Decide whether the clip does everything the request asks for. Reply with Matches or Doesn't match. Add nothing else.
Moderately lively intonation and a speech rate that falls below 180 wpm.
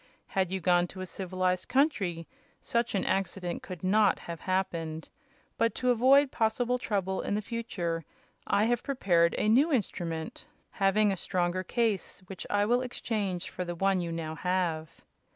Matches